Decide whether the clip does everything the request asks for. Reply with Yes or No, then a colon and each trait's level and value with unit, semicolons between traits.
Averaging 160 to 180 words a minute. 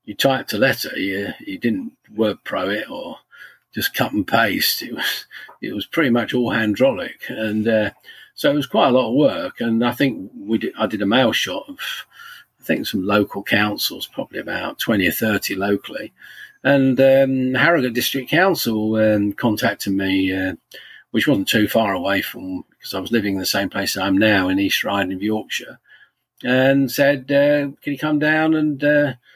No: average, 190 wpm